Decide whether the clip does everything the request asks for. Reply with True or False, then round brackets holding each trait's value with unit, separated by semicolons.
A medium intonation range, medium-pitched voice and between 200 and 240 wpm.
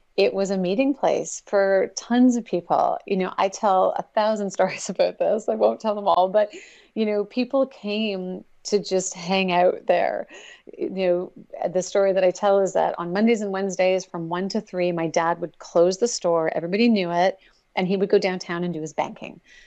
False (3.0 semitones; 195 Hz; 205 wpm)